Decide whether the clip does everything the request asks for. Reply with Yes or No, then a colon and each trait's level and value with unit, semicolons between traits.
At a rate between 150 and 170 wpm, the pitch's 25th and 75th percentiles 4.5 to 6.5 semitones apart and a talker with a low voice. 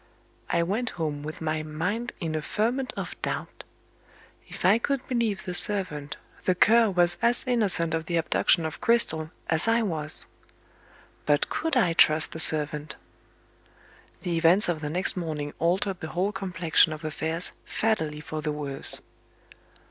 No: average, 155 wpm; average, 5.0 semitones; medium, 170 Hz